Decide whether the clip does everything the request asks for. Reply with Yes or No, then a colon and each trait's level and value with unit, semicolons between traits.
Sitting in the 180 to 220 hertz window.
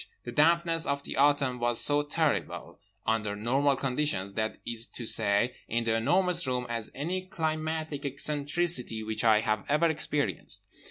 No: medium, 140 Hz